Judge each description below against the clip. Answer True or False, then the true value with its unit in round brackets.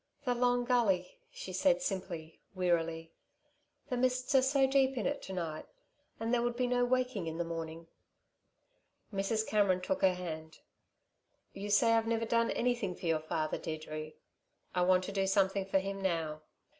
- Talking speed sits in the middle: True (170 wpm)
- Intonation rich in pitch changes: True (6.3 semitones)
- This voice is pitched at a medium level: False (195 Hz)